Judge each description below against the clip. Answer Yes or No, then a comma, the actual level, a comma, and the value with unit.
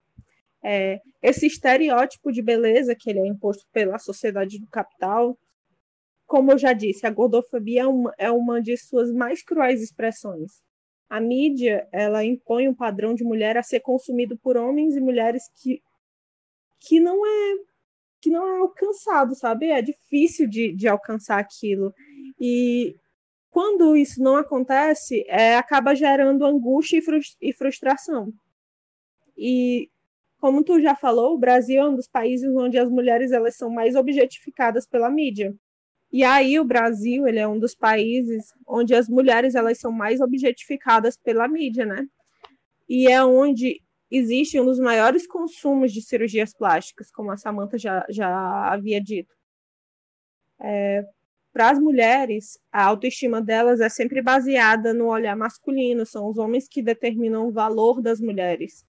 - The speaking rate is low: No, average, 150 wpm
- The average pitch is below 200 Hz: No, high, 245 Hz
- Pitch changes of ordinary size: Yes, average, 3.3 semitones